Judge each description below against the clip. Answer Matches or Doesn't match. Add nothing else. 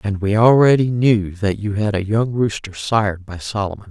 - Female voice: Matches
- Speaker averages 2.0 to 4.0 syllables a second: Doesn't match